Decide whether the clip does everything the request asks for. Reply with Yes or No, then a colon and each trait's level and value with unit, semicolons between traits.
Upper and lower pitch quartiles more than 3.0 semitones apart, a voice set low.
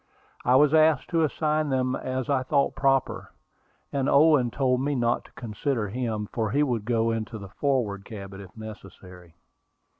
Yes: average, 4.5 semitones; low, 125 Hz